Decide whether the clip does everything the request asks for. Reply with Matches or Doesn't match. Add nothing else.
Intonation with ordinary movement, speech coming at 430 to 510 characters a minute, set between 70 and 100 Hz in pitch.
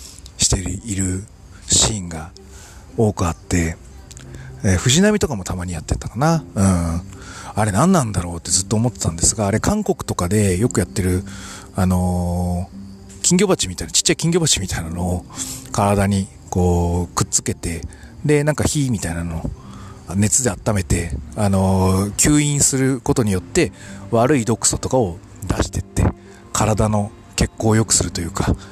Doesn't match